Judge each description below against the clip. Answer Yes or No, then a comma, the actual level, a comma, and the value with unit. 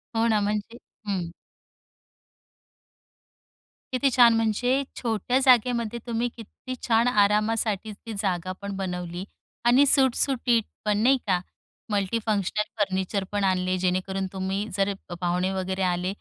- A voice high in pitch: Yes, high, 210 Hz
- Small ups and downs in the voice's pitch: No, average, 3.6 semitones